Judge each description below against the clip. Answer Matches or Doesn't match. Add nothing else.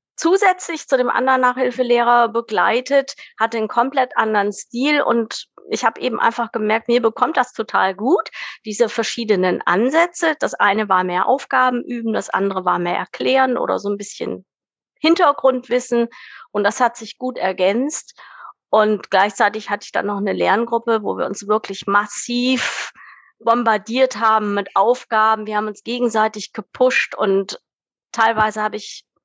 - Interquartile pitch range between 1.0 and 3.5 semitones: Matches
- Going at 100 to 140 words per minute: Doesn't match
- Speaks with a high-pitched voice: Matches